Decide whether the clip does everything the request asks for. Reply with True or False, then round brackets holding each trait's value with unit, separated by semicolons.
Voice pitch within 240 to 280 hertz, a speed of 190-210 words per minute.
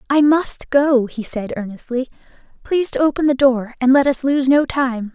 True (265 Hz; 200 wpm)